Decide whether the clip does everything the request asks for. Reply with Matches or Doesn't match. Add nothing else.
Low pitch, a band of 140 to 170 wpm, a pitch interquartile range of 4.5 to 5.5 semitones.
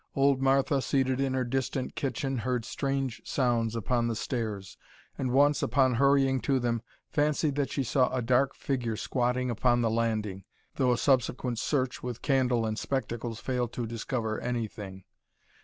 Doesn't match